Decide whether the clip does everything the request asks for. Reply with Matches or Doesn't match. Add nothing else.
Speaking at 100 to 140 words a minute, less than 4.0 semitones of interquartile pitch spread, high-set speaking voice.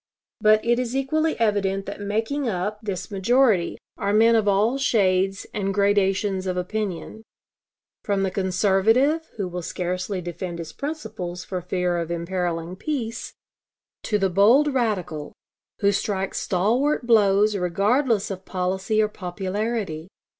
Matches